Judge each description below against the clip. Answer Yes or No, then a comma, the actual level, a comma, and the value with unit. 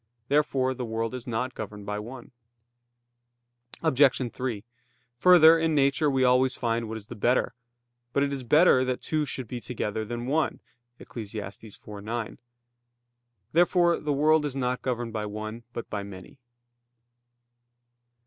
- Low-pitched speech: Yes, low, 125 Hz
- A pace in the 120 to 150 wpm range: Yes, average, 145 wpm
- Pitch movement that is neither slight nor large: Yes, average, 3.9 semitones